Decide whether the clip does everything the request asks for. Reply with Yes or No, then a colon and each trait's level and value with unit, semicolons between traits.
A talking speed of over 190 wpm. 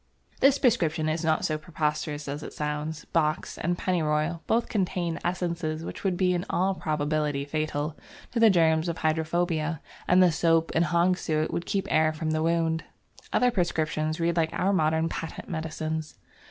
No: average, 170 wpm